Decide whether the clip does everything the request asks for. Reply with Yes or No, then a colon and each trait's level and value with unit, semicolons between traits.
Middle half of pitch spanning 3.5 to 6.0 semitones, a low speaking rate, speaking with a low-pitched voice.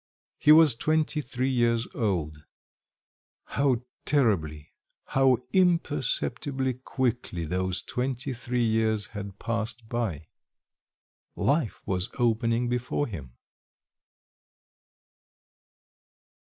Yes: average, 4.2 semitones; slow, 85 wpm; low, 120 Hz